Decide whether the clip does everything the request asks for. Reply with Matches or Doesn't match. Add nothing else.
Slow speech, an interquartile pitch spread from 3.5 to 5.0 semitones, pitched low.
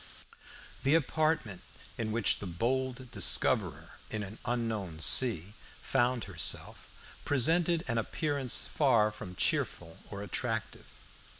Matches